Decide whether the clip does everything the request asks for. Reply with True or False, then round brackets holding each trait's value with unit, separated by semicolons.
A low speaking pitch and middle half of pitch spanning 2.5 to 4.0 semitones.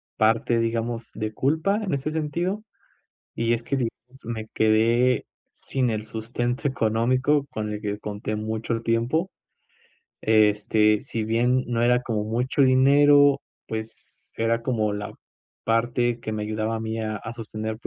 True (115 Hz; 2.8 semitones)